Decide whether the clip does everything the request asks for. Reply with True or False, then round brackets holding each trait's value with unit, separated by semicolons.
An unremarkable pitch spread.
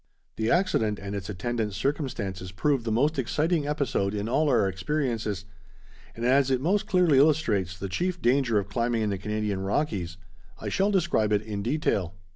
False (6.6 semitones)